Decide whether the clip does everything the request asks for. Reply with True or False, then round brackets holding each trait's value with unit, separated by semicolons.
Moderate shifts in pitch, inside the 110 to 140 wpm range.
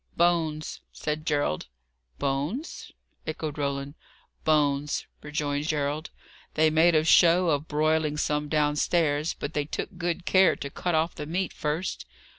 False (2.0 semitones; 135 wpm)